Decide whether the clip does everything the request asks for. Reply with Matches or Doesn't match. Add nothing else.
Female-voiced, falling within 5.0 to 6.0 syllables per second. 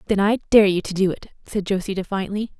Doesn't match